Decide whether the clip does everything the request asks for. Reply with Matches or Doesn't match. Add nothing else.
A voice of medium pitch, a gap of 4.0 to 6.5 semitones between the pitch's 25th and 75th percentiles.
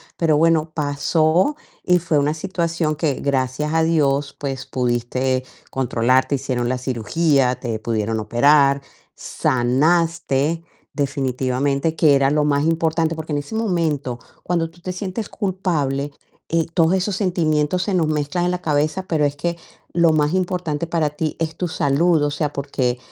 Doesn't match